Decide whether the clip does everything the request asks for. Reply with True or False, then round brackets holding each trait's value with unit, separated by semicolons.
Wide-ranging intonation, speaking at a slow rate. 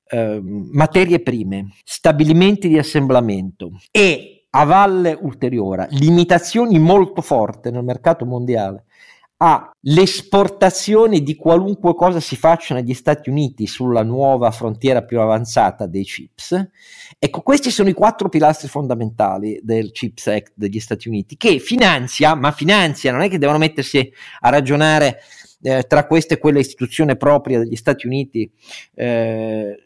False (6.3 semitones; 130 wpm)